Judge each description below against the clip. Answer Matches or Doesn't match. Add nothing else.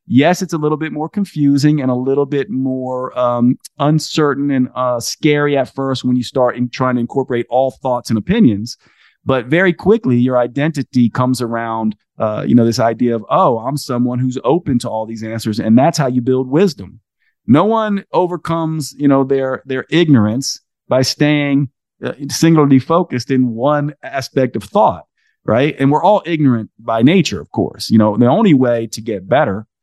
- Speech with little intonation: Doesn't match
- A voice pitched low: Matches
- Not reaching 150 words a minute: Doesn't match